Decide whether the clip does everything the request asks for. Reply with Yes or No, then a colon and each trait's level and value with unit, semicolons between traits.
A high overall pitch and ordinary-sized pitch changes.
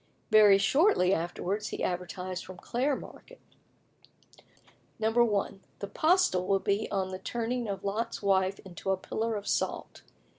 Yes: high, 200 Hz; average, 3.5 semitones